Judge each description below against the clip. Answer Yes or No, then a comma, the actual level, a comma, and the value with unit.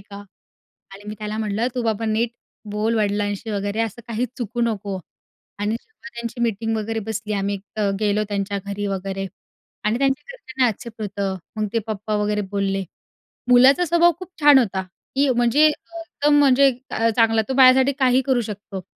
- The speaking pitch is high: Yes, high, 225 Hz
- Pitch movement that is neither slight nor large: Yes, average, 3.8 semitones